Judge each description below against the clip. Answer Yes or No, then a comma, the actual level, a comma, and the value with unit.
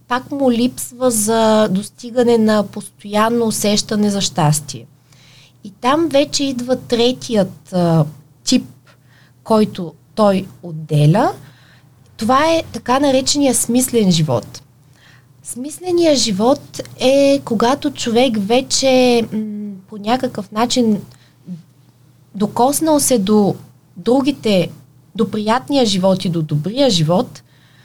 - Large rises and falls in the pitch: Yes, wide, 8.7 semitones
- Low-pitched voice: No, high, 210 Hz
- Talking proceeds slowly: Yes, slow, 95 wpm